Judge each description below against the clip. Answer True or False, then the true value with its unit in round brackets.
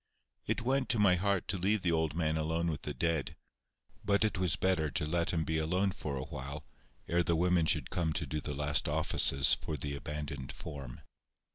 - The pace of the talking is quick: True (210 wpm)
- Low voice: True (80 Hz)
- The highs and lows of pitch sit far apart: False (3.5 semitones)